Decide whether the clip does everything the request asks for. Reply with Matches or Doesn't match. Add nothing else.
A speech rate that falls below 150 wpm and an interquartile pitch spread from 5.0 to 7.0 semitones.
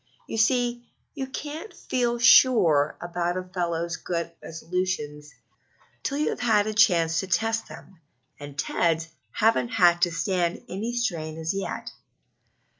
Matches